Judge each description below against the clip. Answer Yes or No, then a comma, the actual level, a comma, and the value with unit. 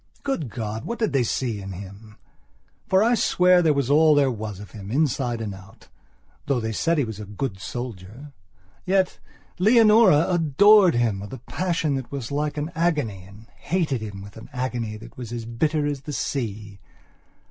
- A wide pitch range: Yes, wide, 6.7 semitones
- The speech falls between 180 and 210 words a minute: Yes, average, 190 wpm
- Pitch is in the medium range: No, low, 130 Hz